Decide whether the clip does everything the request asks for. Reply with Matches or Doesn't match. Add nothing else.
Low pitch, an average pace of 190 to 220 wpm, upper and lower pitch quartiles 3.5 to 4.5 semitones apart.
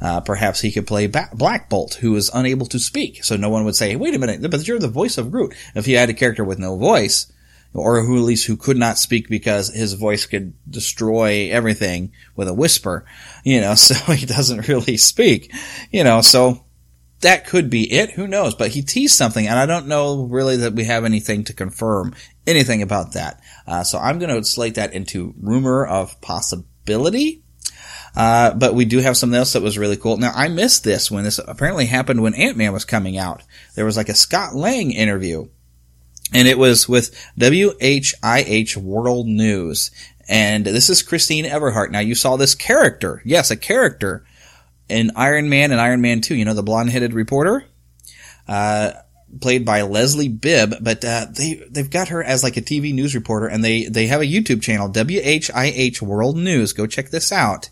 Matches